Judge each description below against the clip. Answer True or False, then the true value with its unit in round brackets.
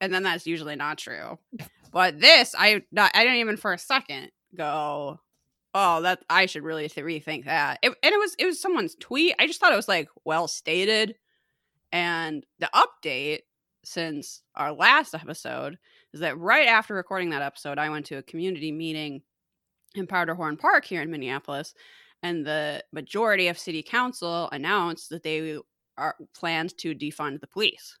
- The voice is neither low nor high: True (170 Hz)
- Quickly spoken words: False (175 wpm)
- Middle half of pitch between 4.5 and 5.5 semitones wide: True (5.1 semitones)